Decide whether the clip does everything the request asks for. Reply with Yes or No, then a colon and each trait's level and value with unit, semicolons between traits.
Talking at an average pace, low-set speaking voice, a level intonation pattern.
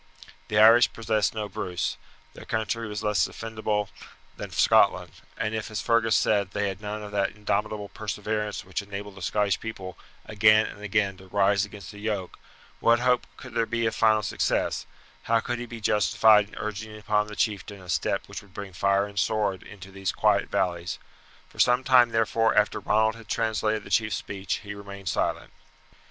Yes: average, 185 wpm; low, 105 Hz; narrow, 1.7 semitones